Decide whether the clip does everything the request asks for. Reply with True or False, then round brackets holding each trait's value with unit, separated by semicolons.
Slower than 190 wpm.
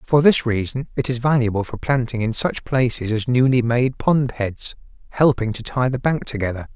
False (195 wpm)